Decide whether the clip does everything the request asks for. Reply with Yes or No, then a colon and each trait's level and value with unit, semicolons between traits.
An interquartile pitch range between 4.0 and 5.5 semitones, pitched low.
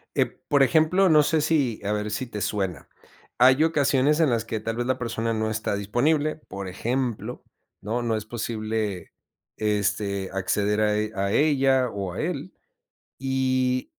Yes: average, 4.4 semitones; low, 115 Hz